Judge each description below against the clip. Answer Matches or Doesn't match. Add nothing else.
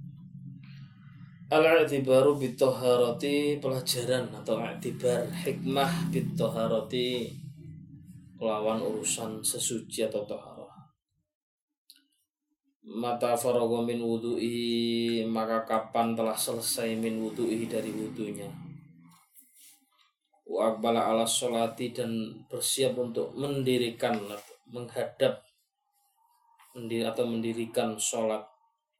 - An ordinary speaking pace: Doesn't match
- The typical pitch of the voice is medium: Doesn't match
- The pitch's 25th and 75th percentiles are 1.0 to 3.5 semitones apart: Doesn't match